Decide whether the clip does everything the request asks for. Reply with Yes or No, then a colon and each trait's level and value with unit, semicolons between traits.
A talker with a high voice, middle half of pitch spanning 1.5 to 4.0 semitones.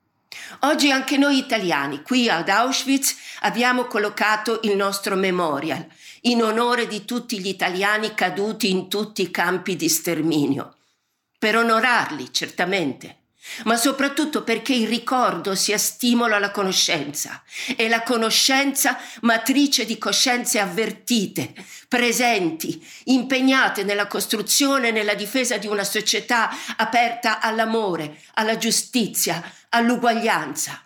Yes: high, 225 Hz; average, 3.3 semitones